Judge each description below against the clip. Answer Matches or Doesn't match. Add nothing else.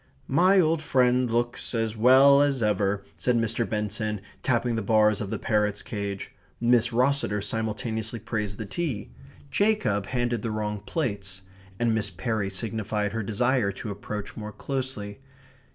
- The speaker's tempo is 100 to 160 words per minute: Matches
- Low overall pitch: Matches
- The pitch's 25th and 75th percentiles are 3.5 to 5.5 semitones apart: Doesn't match